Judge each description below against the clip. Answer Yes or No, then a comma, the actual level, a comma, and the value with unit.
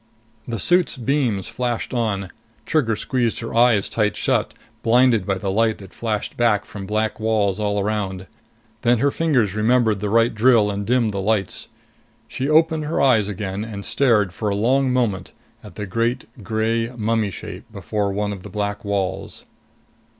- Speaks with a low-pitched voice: Yes, low, 110 Hz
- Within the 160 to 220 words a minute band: Yes, average, 170 wpm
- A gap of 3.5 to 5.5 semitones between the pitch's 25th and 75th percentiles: No, average, 2.9 semitones